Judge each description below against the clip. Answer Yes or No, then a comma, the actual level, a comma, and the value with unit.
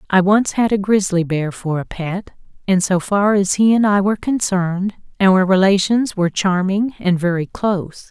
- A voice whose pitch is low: No, high, 190 Hz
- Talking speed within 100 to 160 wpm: No, average, 185 wpm